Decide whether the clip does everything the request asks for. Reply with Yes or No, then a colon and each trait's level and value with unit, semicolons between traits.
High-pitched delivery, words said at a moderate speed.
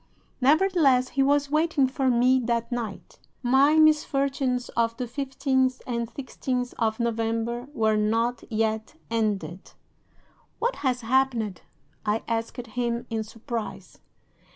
No: high, 245 Hz; slow, 120 wpm